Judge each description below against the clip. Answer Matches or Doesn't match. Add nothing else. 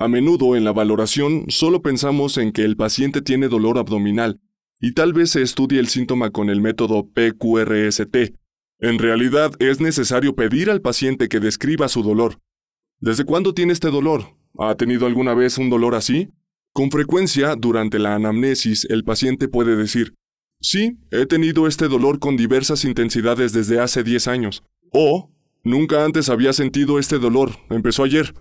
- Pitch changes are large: Doesn't match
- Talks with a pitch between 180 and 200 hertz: Doesn't match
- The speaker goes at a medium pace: Matches